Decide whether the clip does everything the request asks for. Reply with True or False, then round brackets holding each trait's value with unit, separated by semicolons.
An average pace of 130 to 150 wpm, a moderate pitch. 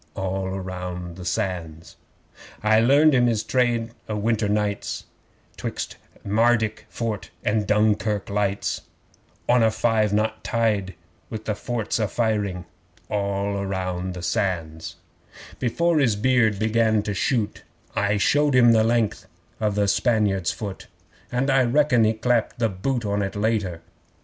False (140 wpm; 105 Hz)